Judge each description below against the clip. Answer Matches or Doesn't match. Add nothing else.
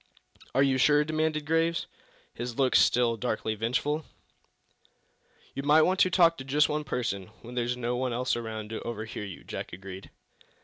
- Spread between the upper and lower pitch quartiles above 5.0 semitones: Doesn't match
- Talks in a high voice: Doesn't match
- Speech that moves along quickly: Doesn't match